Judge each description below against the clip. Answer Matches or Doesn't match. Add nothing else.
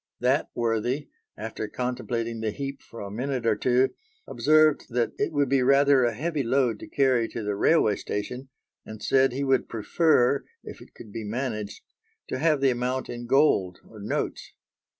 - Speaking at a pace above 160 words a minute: Matches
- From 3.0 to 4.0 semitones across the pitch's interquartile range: Matches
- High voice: Doesn't match